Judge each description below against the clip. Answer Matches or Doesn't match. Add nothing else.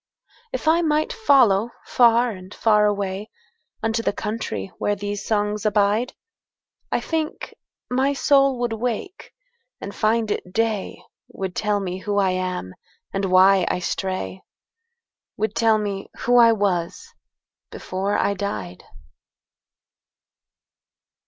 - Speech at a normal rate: Doesn't match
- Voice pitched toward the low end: Doesn't match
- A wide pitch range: Doesn't match